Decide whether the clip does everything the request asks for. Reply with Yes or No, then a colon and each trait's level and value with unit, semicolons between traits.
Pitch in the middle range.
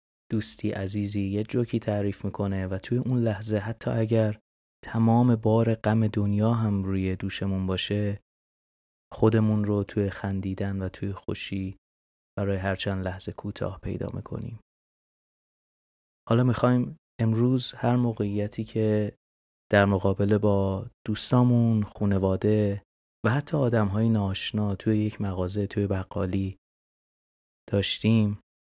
No: low, 105 Hz